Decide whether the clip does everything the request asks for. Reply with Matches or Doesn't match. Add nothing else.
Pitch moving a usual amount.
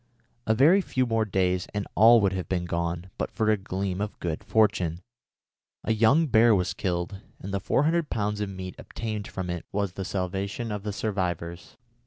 Matches